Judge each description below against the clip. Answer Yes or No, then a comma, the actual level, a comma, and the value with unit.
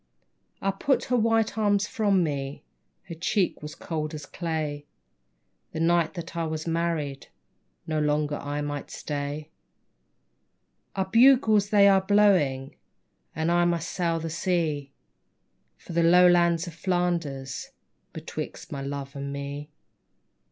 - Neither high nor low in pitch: Yes, medium, 165 Hz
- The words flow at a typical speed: No, slow, 130 wpm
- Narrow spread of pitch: No, average, 4.2 semitones